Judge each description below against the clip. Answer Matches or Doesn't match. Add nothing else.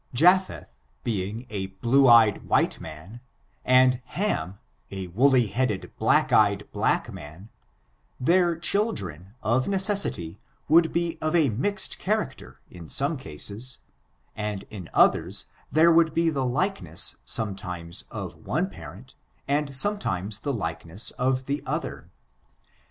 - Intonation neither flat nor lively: Doesn't match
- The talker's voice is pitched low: Matches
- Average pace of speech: Doesn't match